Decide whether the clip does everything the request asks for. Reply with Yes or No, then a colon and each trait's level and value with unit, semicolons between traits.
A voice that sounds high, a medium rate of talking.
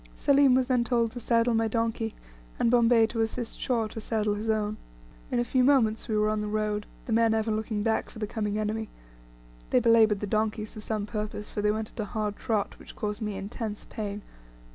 No: high, 220 Hz; fast, 220 wpm